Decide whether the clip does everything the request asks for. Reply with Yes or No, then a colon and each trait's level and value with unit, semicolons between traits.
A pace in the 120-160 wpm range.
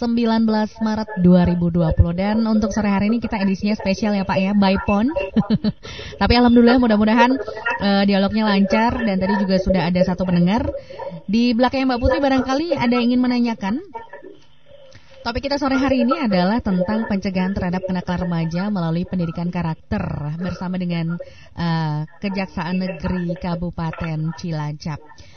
Yes: fast, 140 wpm